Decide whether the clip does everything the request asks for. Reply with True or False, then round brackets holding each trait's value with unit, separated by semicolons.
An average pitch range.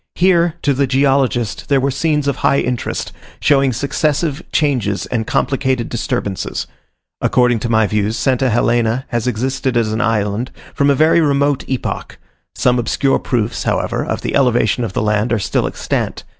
True (3.5 semitones)